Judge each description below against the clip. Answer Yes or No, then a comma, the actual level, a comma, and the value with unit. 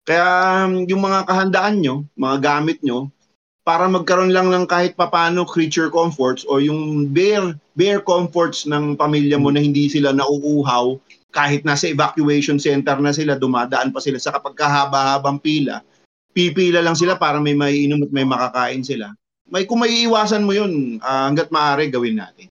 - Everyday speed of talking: No, fast, 165 wpm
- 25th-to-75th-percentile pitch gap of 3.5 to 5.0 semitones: Yes, average, 4.1 semitones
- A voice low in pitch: No, medium, 150 Hz